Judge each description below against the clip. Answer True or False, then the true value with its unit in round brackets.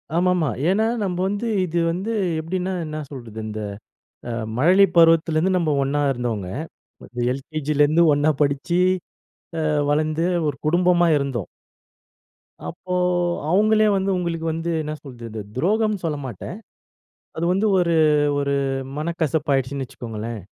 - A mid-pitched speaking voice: True (160 Hz)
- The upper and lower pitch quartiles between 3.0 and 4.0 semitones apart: False (4.4 semitones)